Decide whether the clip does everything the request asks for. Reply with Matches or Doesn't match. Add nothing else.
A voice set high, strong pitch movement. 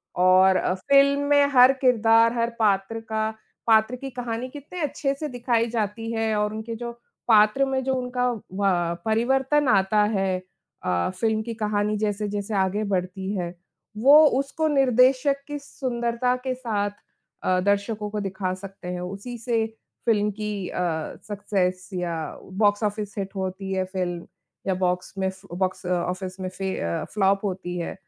Doesn't match